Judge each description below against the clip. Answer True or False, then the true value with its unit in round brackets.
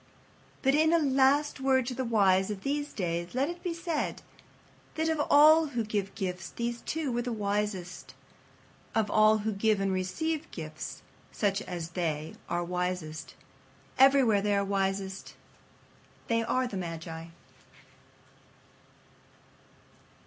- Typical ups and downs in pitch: False (6.4 semitones)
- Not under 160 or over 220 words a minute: False (135 wpm)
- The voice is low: False (215 Hz)